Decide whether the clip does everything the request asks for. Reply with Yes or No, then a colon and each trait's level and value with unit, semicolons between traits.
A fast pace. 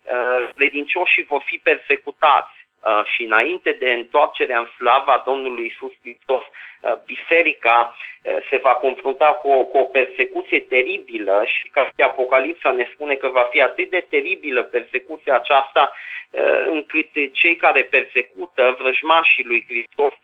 No: average, 130 wpm